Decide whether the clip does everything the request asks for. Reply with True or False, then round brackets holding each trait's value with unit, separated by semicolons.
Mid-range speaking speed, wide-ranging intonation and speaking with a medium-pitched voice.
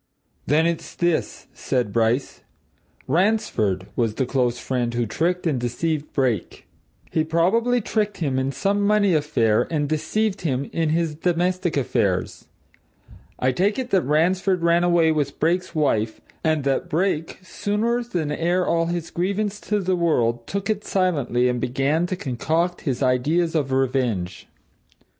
True (150 wpm; 5.9 semitones; 160 Hz)